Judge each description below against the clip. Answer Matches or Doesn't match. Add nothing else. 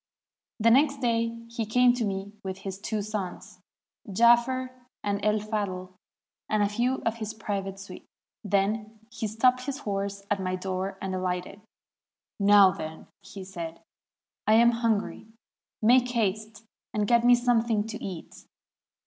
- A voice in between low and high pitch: Doesn't match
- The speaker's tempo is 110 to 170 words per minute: Matches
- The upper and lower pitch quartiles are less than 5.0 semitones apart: Matches